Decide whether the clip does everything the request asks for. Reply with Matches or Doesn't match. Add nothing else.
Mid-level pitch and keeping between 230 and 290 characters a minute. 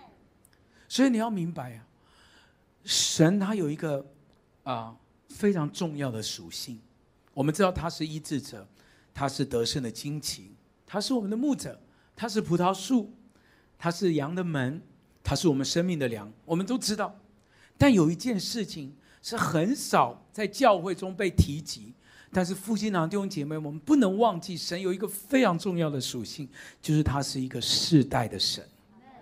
Matches